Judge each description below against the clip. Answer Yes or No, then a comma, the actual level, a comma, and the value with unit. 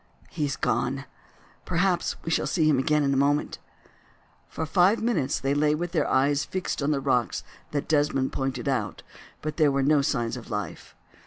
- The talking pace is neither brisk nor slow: Yes, average, 185 wpm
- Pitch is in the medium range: Yes, medium, 145 Hz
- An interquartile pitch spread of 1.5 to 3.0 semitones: Yes, narrow, 2.5 semitones